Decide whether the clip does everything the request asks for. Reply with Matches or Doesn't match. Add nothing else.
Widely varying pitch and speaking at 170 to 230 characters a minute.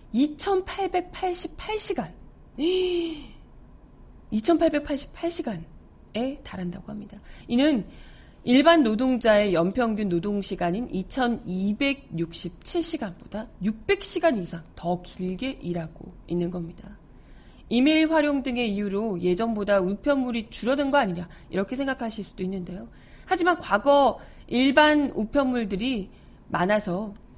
Matches